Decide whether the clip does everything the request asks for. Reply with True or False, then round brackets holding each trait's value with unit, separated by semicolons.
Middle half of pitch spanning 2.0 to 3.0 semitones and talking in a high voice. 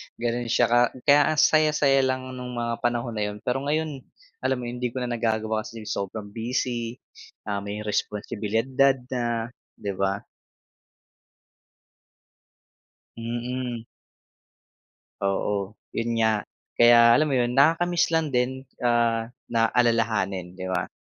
False (2.5 semitones; 120 Hz)